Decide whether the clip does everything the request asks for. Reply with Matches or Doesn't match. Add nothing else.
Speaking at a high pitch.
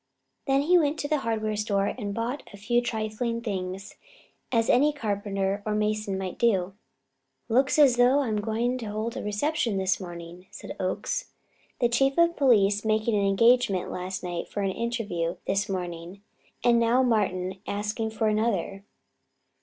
Matches